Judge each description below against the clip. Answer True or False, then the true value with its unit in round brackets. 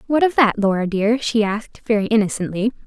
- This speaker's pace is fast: False (190 wpm)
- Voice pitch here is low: False (220 Hz)